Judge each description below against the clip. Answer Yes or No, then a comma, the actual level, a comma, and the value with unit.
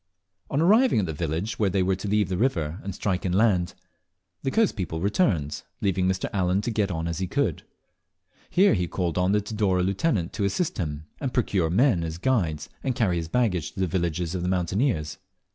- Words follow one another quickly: Yes, fast, 210 wpm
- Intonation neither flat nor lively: Yes, average, 4.0 semitones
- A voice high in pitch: No, very low, 95 Hz